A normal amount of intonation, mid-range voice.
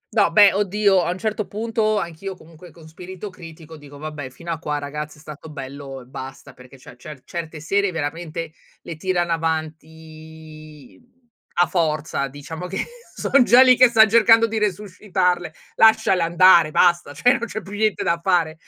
Yes: average, 4.3 semitones; medium, 170 Hz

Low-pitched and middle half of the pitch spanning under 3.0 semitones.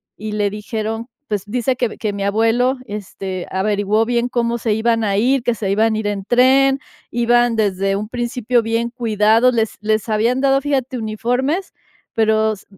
No: high, 225 Hz; narrow, 2.5 semitones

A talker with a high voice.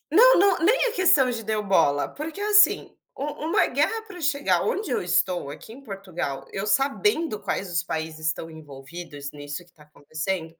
Yes: high, 195 Hz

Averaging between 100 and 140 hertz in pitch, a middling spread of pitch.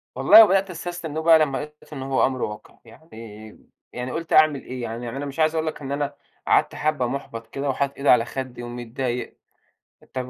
Yes: low, 135 Hz; average, 4.1 semitones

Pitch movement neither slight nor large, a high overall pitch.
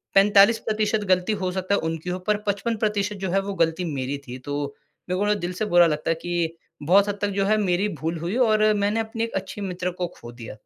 Yes: average, 3.3 semitones; high, 195 Hz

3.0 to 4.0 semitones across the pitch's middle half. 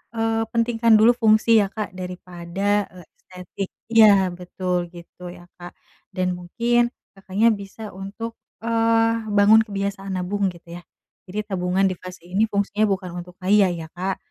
Yes: average, 3.3 semitones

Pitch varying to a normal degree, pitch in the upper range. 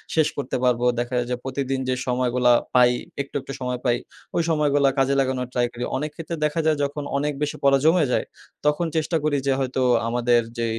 No: average, 3.1 semitones; low, 135 Hz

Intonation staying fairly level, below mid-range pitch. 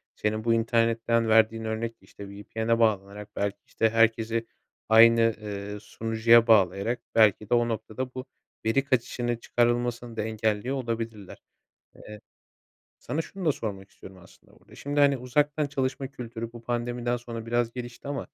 Yes: narrow, 1.7 semitones; low, 115 Hz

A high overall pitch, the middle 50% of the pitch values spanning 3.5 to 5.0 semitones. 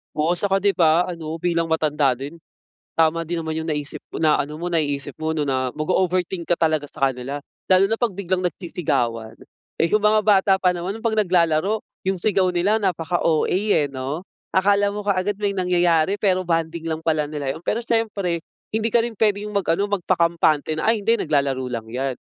No: medium, 170 Hz; average, 4.0 semitones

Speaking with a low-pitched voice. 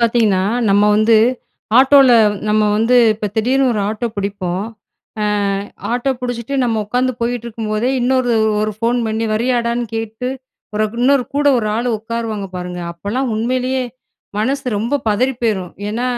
No: high, 230 Hz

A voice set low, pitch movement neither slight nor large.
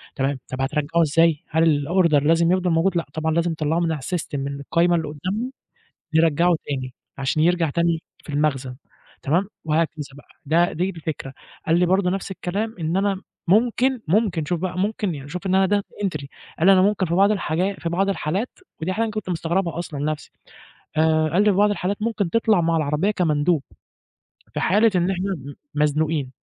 No: medium, 170 Hz; average, 3.8 semitones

